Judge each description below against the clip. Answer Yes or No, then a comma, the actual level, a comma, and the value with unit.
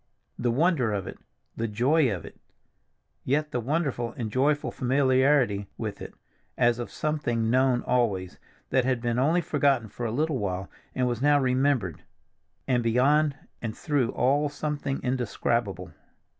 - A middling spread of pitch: Yes, average, 3.7 semitones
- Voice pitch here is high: No, low, 125 Hz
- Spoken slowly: No, average, 145 wpm